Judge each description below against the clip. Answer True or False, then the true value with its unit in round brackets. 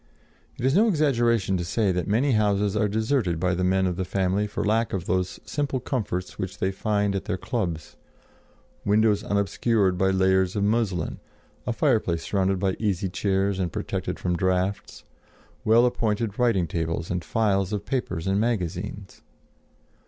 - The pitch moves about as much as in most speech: True (3.0 semitones)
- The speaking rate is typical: True (165 wpm)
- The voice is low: True (100 Hz)